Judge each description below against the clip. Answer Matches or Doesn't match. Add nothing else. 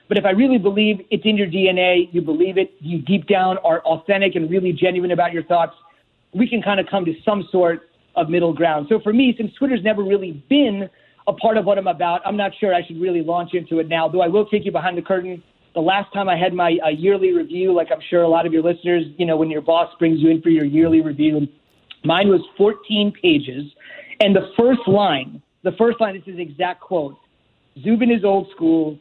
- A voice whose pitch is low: Doesn't match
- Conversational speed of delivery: Doesn't match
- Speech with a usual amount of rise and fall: Matches